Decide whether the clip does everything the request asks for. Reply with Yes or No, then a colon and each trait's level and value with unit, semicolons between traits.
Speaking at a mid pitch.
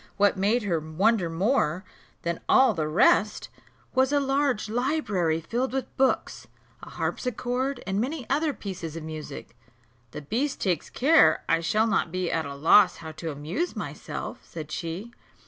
No: high, 200 Hz